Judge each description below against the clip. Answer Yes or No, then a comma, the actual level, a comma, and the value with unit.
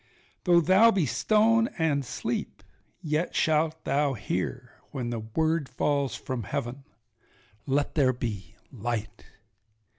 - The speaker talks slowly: Yes, slow, 115 wpm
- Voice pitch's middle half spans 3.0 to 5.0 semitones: No, wide, 5.4 semitones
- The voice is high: No, medium, 140 Hz